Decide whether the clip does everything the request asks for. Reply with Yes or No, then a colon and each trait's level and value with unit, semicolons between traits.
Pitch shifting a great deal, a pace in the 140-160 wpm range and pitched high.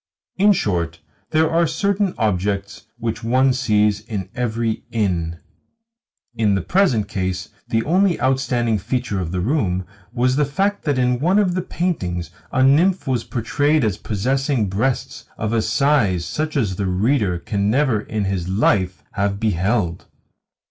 No: wide, 6.0 semitones; average, 155 wpm; low, 115 Hz